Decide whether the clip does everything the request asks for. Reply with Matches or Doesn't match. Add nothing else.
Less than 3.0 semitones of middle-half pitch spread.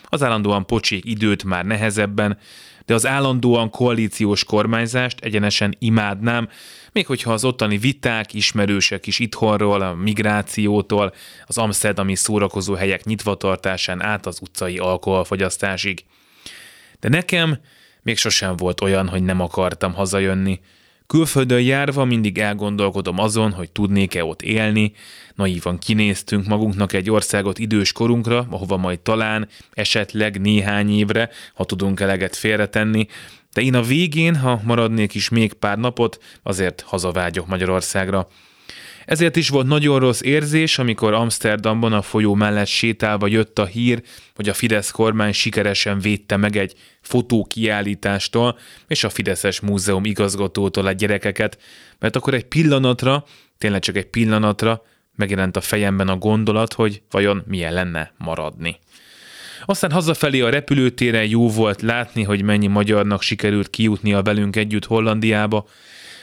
Matches